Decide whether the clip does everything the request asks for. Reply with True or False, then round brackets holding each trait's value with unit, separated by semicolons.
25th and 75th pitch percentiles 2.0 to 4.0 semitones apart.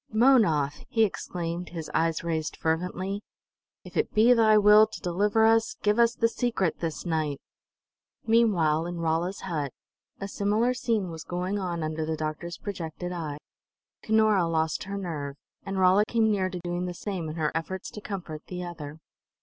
False (4.5 semitones)